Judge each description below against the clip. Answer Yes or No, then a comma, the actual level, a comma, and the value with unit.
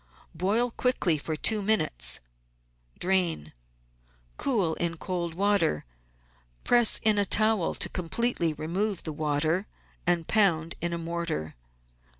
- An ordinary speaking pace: No, slow, 125 wpm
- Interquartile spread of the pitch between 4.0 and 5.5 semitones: Yes, average, 4.4 semitones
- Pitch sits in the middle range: Yes, medium, 175 Hz